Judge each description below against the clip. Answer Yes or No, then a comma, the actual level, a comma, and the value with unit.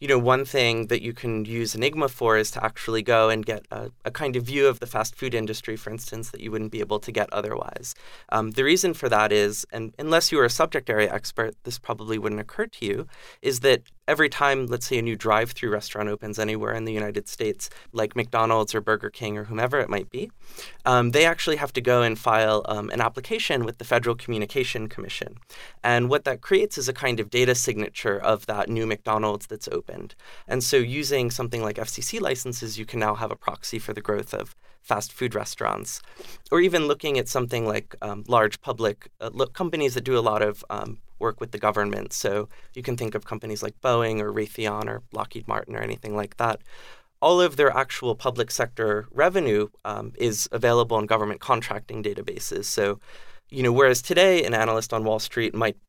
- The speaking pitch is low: Yes, low, 115 Hz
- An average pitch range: Yes, average, 3.1 semitones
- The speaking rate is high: Yes, fast, 215 wpm